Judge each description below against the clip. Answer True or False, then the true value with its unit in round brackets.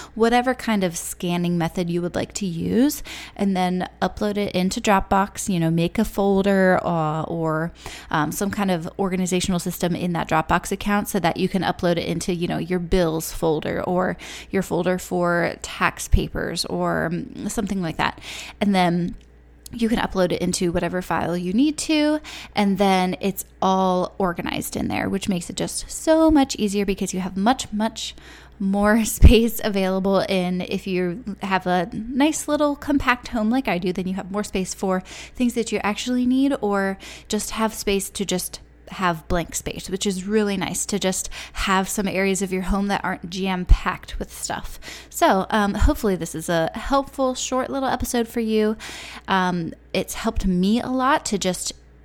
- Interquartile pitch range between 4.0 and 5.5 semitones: False (3.2 semitones)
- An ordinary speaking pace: True (185 wpm)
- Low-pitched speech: False (195 Hz)